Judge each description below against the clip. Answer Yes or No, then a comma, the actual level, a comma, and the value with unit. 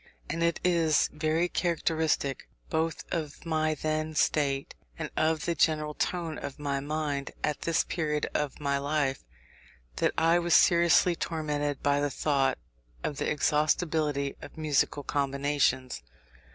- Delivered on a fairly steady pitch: Yes, narrow, 2.1 semitones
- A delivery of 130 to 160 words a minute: Yes, average, 140 wpm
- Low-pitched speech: No, medium, 150 Hz